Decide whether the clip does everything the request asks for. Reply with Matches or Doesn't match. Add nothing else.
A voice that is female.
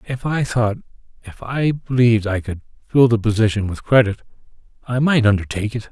Doesn't match